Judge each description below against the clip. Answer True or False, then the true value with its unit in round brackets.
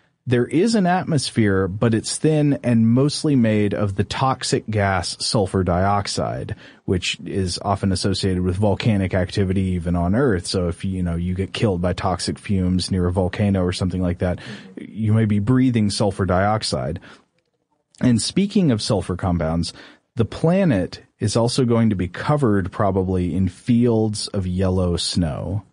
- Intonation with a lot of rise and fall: False (4.6 semitones)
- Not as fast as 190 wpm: True (160 wpm)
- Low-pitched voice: True (105 Hz)